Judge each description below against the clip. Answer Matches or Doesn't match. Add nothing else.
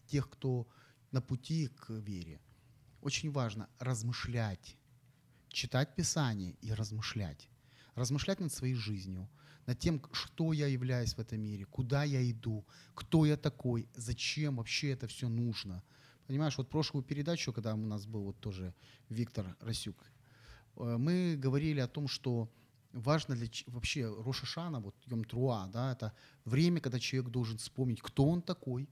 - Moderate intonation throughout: Matches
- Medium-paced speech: Matches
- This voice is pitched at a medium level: Doesn't match